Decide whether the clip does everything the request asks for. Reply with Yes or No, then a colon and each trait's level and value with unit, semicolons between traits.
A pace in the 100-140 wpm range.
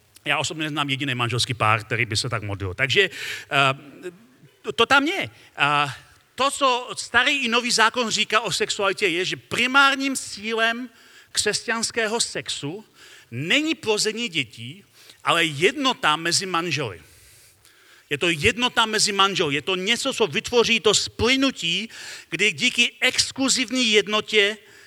Yes: average, 130 wpm